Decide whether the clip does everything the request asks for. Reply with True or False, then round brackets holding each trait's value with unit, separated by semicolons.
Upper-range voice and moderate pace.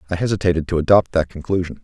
False (90 Hz; 195 wpm)